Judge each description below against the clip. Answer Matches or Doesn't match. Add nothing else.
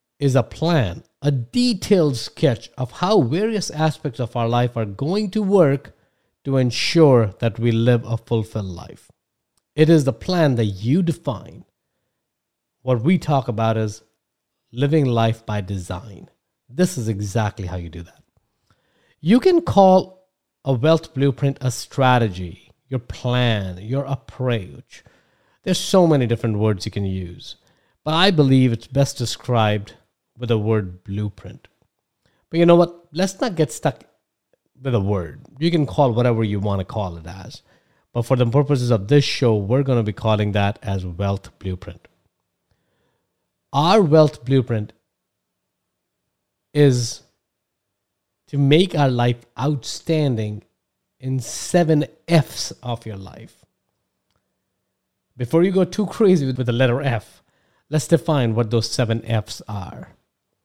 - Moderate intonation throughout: Doesn't match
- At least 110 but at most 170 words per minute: Matches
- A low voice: Matches